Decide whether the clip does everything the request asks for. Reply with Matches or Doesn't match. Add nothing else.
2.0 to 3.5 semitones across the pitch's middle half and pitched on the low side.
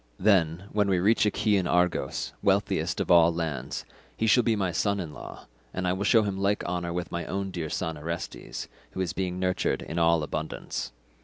Matches